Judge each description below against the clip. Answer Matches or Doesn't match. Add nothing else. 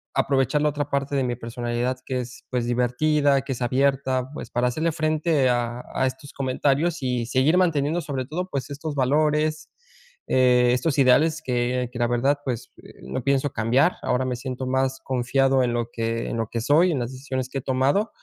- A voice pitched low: Matches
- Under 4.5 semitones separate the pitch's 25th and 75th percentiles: Matches